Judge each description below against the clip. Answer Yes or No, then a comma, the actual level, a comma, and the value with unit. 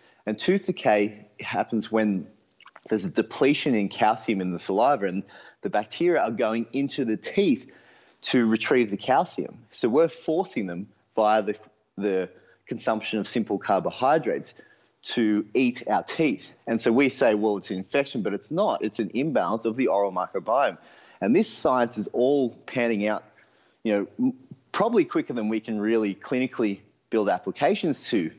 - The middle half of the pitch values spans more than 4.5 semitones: No, average, 3.3 semitones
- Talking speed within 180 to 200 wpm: No, average, 165 wpm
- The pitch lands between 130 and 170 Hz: No, low, 110 Hz